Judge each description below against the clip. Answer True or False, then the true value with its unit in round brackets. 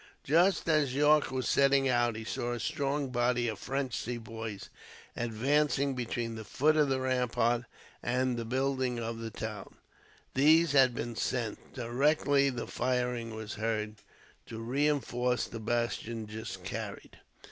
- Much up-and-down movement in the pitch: False (3.2 semitones)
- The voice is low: True (125 Hz)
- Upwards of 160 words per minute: False (145 wpm)